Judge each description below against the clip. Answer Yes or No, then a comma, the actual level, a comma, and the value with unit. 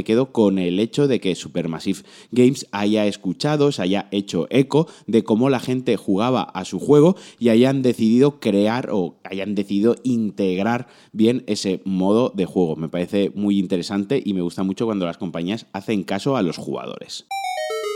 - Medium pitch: No, low, 105 Hz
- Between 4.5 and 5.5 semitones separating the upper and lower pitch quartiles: Yes, average, 4.9 semitones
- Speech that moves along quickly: No, average, 175 wpm